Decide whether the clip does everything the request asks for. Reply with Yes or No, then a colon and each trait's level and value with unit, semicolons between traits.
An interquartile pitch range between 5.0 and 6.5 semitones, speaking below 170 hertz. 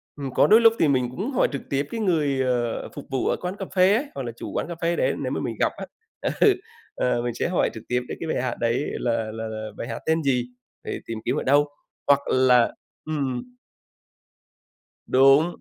Yes: wide, 5.5 semitones; low, 135 Hz